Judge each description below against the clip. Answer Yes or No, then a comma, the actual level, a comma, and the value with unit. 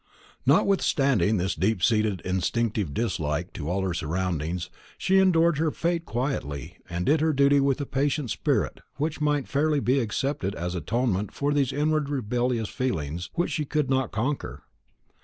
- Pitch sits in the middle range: No, low, 125 Hz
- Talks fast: No, average, 160 wpm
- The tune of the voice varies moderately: No, wide, 7.7 semitones